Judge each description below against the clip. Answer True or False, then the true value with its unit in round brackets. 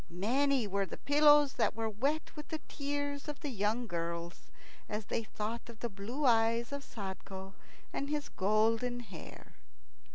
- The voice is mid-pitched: False (230 Hz)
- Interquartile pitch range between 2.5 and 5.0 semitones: False (5.4 semitones)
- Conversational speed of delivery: True (160 wpm)